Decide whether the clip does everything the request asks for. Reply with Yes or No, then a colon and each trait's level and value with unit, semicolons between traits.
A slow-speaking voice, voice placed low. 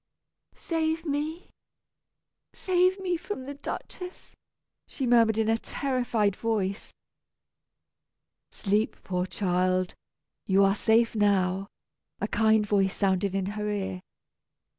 No: slow, 110 wpm; high, 215 Hz